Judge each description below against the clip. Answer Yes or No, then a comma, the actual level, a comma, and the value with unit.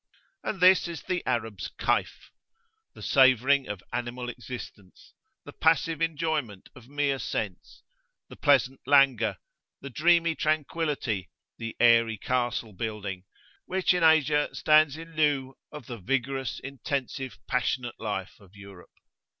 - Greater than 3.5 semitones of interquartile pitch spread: Yes, average, 4.9 semitones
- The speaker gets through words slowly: Yes, slow, 125 wpm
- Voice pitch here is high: No, low, 130 Hz